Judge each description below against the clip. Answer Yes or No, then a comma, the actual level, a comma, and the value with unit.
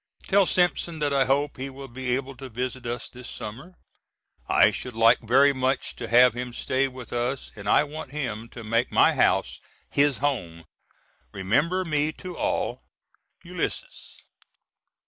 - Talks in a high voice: No, low, 130 Hz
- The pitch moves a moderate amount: Yes, average, 3.3 semitones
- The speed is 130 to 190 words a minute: Yes, average, 160 wpm